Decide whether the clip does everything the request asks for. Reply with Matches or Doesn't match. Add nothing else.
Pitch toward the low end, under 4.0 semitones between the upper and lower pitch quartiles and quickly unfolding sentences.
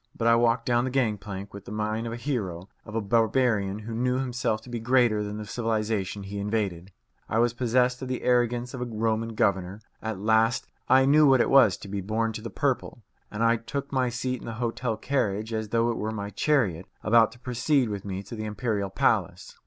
Matches